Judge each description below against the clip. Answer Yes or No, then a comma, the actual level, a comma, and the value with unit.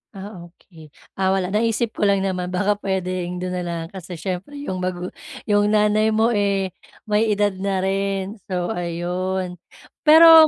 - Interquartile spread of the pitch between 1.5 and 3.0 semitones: Yes, narrow, 2.4 semitones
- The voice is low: No, high, 190 Hz